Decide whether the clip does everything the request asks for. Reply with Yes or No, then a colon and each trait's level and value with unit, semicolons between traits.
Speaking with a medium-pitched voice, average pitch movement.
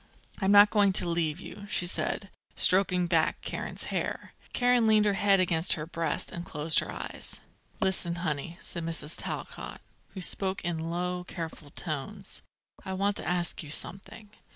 Yes: medium, 180 Hz; average, 3.0 semitones